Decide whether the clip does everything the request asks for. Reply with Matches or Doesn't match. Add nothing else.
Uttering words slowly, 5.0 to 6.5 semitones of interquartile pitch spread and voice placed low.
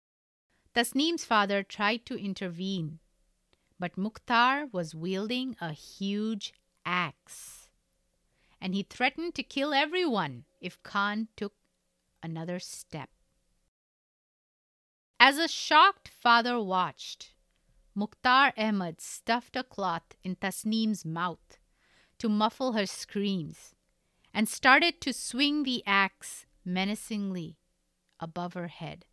Doesn't match